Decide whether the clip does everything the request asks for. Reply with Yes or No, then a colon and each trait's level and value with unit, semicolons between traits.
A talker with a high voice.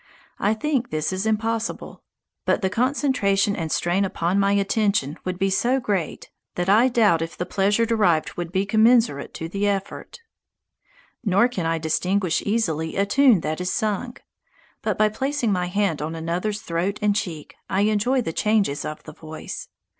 Yes: high, 200 Hz